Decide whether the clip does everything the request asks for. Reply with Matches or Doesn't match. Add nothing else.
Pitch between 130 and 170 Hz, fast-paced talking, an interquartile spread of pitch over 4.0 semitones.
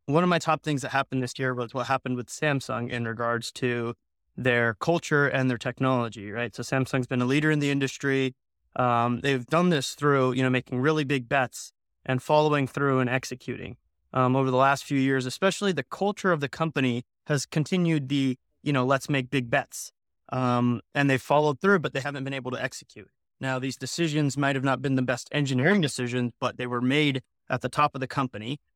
Doesn't match